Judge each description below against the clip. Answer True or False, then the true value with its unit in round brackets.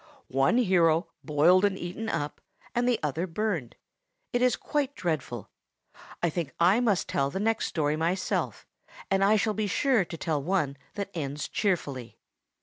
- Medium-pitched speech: True (180 Hz)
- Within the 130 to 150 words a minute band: False (160 wpm)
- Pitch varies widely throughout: True (5.8 semitones)